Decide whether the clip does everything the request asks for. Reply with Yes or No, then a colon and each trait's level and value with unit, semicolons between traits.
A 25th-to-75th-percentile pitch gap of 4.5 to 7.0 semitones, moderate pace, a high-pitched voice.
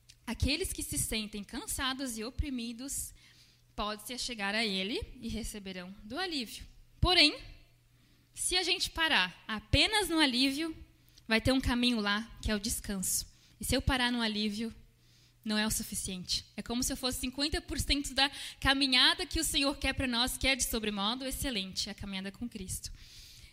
Yes: average, 5.0 semitones; average, 165 wpm; high, 235 Hz